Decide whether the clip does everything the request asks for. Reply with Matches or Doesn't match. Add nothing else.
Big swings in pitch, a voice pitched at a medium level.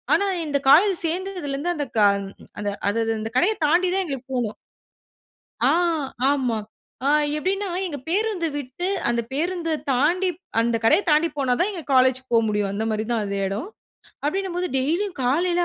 Doesn't match